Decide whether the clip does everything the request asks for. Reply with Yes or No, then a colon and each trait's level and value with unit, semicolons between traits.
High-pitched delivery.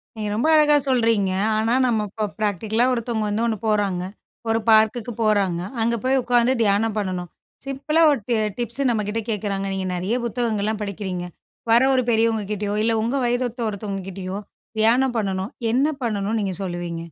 Yes: high, 220 Hz